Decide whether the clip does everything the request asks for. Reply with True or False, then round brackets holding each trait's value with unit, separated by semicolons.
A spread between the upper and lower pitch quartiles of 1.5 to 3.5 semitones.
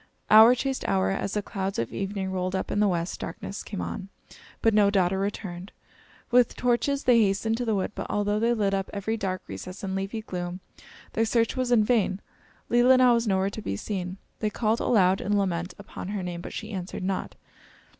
True (3.0 semitones)